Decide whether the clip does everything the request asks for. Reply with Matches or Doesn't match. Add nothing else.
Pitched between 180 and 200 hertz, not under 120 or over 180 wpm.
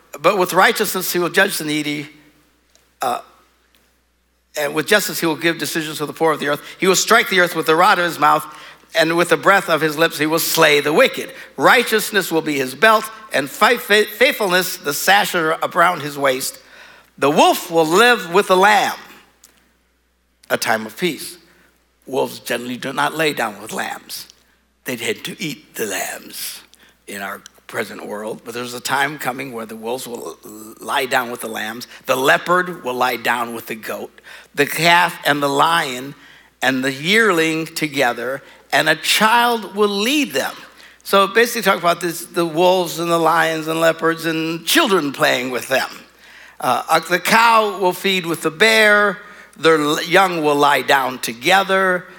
Doesn't match